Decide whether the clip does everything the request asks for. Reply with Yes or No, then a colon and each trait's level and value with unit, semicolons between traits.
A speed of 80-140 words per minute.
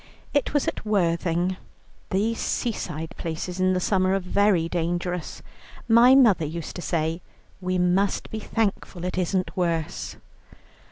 Yes: slow, 135 wpm